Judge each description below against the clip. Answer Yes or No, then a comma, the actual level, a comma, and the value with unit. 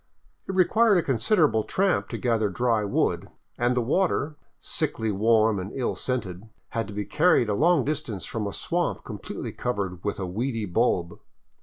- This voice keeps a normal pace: Yes, average, 170 wpm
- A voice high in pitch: No, low, 115 Hz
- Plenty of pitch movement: Yes, wide, 6.0 semitones